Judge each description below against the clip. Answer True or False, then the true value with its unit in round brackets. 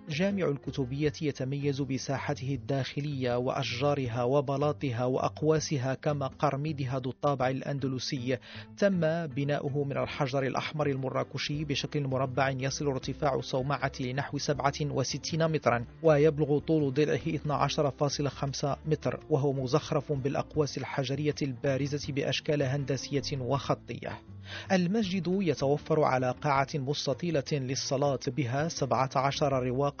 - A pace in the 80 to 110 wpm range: True (100 wpm)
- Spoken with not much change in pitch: True (1.9 semitones)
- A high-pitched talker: False (140 Hz)